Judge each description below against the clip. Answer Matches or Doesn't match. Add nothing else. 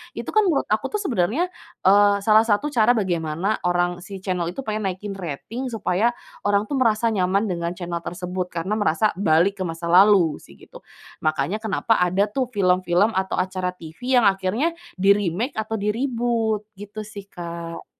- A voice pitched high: Matches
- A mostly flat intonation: Doesn't match